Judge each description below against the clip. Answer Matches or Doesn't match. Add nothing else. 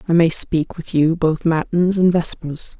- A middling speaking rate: Matches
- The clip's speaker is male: Doesn't match